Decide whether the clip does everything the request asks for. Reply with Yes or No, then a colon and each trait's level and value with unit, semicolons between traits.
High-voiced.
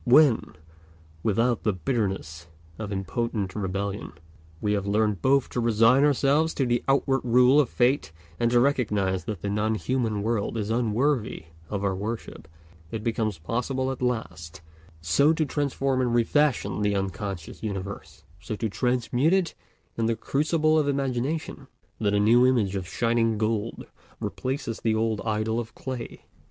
No: low, 115 Hz